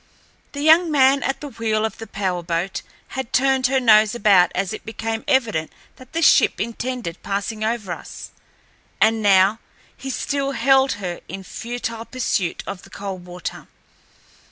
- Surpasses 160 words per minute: No, average, 155 wpm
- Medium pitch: No, high, 225 Hz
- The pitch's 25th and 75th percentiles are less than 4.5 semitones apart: No, average, 5.2 semitones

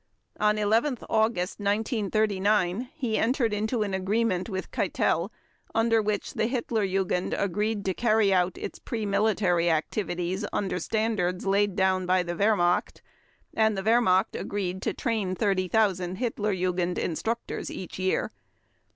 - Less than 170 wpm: Yes, slow, 135 wpm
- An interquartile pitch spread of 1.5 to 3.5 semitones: Yes, average, 3.0 semitones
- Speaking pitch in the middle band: No, high, 205 Hz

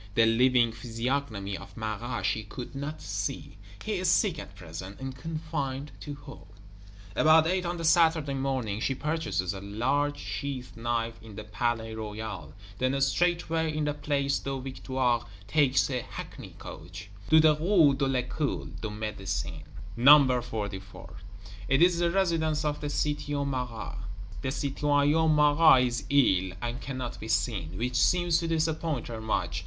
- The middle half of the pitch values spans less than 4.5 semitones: No, average, 5.2 semitones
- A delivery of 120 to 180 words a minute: Yes, average, 155 wpm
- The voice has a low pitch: Yes, low, 130 Hz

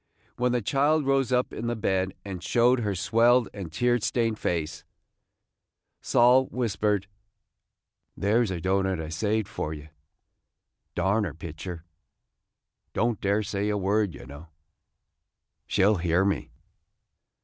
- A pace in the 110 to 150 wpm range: Yes, average, 140 wpm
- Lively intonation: No, average, 4.3 semitones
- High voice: No, low, 100 Hz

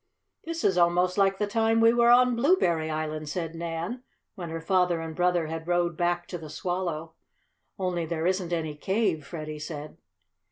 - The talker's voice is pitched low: No, medium, 175 Hz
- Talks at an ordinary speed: Yes, average, 175 wpm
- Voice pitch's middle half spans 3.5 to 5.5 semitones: No, average, 3.1 semitones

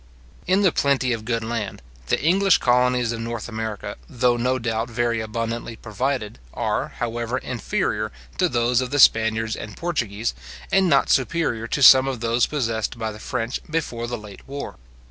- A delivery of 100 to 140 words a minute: No, average, 170 wpm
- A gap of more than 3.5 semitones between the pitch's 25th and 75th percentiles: No, average, 2.7 semitones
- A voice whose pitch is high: No, low, 120 Hz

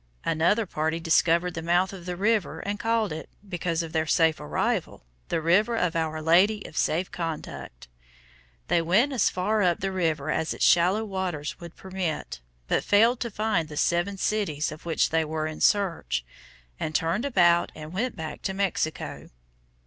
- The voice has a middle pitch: Yes, medium, 175 Hz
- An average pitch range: Yes, average, 3.7 semitones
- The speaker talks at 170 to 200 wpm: Yes, average, 175 wpm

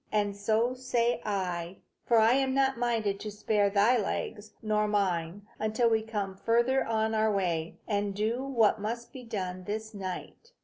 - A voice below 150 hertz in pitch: No, high, 215 Hz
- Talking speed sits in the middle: Yes, average, 170 wpm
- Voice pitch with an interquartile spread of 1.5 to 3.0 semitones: Yes, narrow, 2.6 semitones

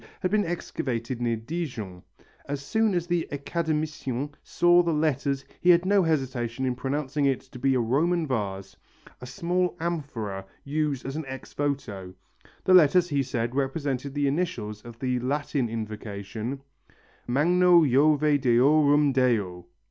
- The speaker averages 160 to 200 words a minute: No, average, 145 wpm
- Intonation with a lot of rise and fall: No, average, 4.7 semitones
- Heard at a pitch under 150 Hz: Yes, medium, 140 Hz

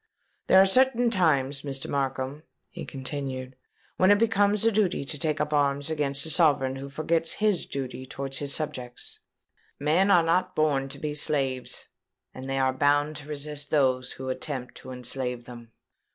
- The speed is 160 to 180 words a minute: Yes, average, 170 wpm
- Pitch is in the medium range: Yes, medium, 145 Hz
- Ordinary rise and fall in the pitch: Yes, average, 3.4 semitones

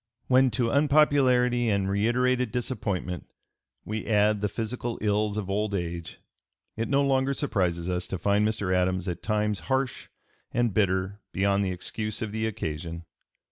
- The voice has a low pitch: Yes, low, 105 Hz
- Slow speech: No, average, 150 wpm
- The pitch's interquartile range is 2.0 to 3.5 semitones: No, average, 4.3 semitones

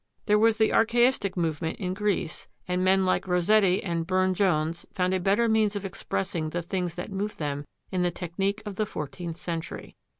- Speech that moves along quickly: No, average, 190 wpm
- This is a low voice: No, medium, 185 Hz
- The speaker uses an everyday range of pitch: Yes, average, 3.0 semitones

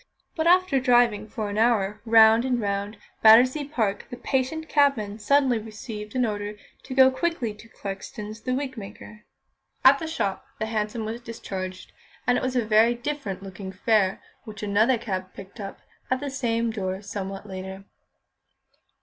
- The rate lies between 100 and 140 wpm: No, average, 160 wpm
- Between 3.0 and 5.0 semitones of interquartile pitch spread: Yes, average, 3.9 semitones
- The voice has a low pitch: No, high, 220 Hz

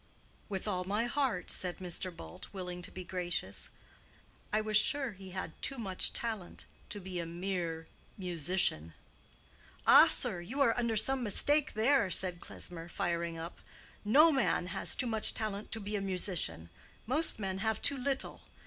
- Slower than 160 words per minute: No, average, 165 wpm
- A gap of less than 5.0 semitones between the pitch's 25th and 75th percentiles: Yes, average, 4.1 semitones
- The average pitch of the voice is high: Yes, high, 195 Hz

